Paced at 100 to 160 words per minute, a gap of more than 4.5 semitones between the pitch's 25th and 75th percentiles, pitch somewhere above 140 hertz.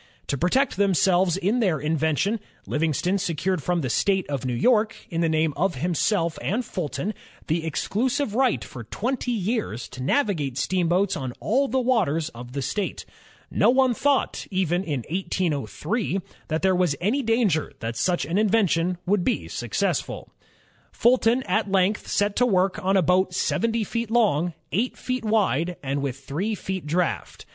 No: average, 170 wpm; wide, 5.6 semitones; medium, 185 Hz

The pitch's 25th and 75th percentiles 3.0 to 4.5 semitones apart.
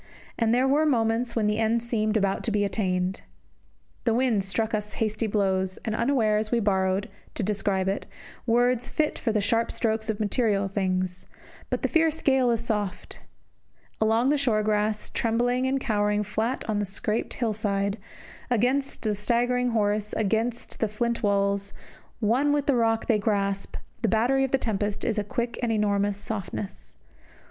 No: narrow, 2.6 semitones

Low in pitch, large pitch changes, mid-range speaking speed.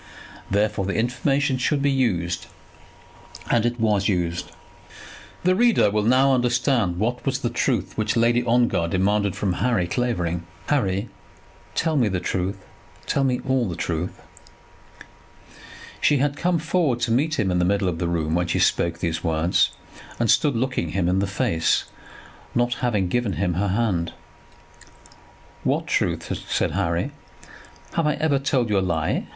Yes: low, 110 Hz; wide, 6.1 semitones; average, 160 wpm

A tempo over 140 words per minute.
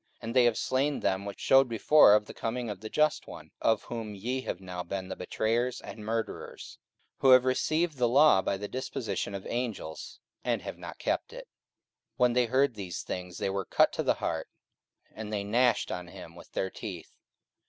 Yes: fast, 205 wpm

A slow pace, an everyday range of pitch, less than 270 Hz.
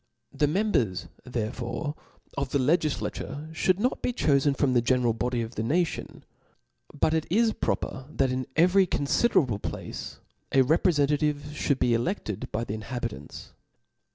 No: average, 150 wpm; average, 4.8 semitones; medium, 140 Hz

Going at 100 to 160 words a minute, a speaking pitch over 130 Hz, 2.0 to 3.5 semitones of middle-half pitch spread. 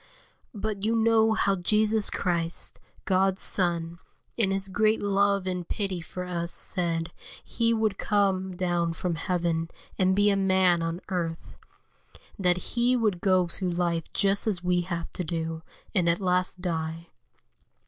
Yes: average, 150 wpm; medium, 185 Hz; average, 2.8 semitones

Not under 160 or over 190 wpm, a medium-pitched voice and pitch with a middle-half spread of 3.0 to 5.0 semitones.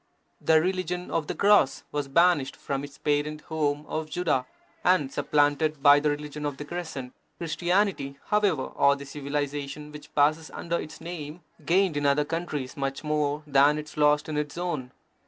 No: average, 170 wpm; medium, 150 Hz; narrow, 2.4 semitones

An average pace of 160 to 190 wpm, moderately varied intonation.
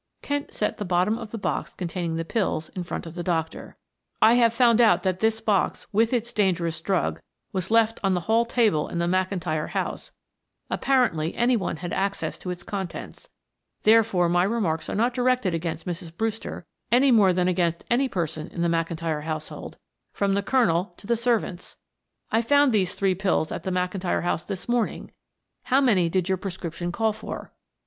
Yes: average, 185 wpm; average, 4.6 semitones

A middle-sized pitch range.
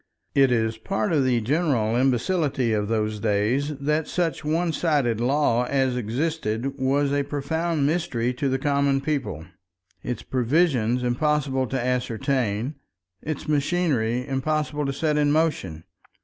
Yes: average, 3.9 semitones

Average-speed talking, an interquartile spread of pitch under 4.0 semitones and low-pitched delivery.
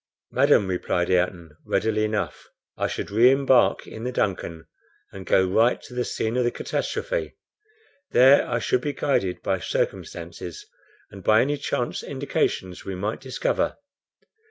No: average, 150 wpm; wide, 5.4 semitones; low, 110 Hz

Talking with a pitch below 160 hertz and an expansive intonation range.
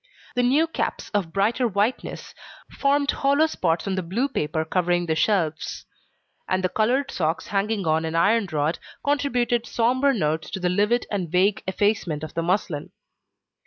No: high, 195 Hz; wide, 6.4 semitones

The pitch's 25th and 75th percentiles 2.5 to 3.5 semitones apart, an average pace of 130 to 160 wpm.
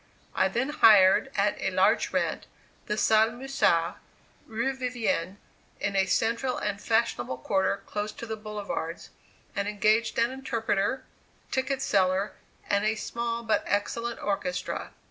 Yes: average, 2.9 semitones; slow, 135 wpm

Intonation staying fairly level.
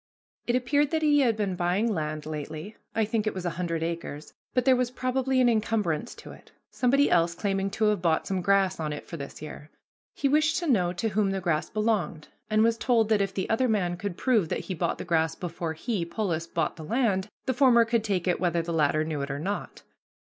No: wide, 5.6 semitones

